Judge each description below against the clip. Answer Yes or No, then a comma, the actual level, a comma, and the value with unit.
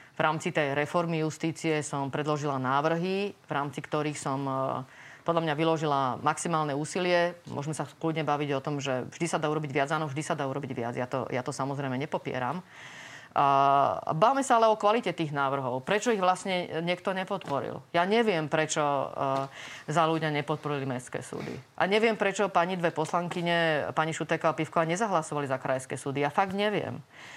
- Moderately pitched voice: Yes, medium, 155 Hz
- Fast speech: Yes, fast, 170 wpm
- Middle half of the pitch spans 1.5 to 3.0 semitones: No, average, 3.6 semitones